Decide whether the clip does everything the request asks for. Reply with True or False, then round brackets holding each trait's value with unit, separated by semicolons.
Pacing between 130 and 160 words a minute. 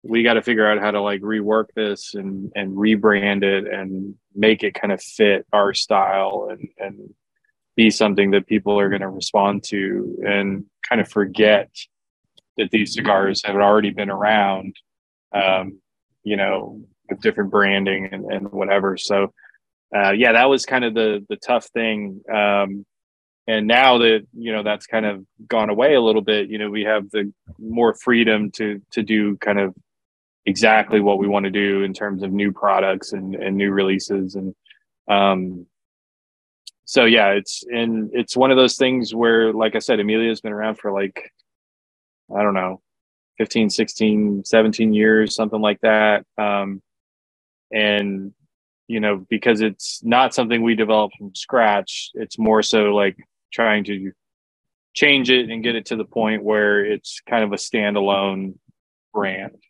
False (170 wpm)